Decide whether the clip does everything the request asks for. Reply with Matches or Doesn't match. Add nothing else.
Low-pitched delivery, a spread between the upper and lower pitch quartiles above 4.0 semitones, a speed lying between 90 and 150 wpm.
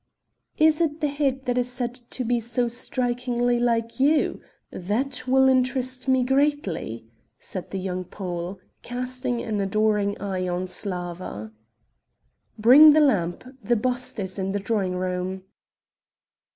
Doesn't match